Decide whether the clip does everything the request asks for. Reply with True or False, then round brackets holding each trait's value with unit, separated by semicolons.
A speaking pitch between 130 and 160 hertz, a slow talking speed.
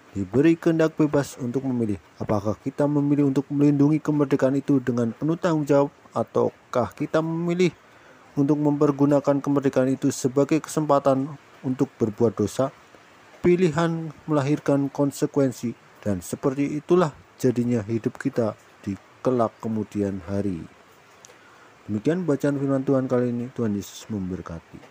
True (135 Hz; 120 wpm)